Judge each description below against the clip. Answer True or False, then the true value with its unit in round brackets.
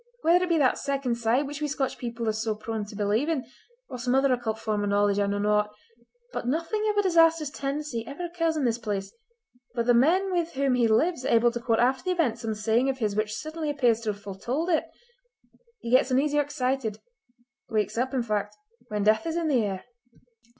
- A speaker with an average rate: False (220 wpm)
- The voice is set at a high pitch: True (250 Hz)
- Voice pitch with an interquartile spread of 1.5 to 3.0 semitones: False (5.5 semitones)